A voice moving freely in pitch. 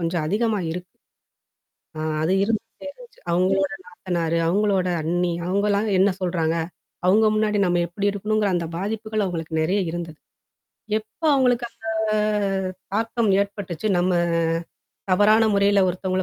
No: average, 3.4 semitones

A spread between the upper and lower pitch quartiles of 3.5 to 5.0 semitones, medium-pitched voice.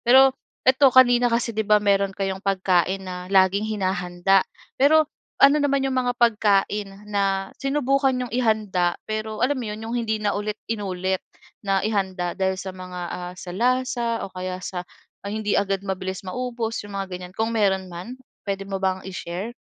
No: average, 3.8 semitones; high, 200 Hz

